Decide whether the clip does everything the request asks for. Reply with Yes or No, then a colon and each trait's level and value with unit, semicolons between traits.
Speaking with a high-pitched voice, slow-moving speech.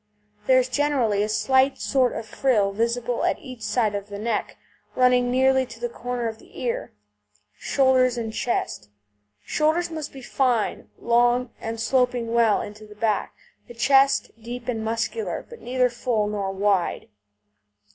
No: high, 240 Hz; average, 155 wpm